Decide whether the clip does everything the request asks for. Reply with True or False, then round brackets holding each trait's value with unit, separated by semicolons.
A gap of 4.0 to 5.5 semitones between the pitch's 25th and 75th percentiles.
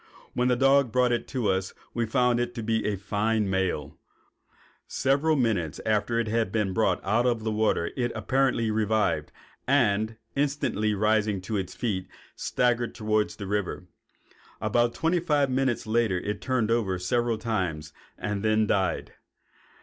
False (3.0 semitones)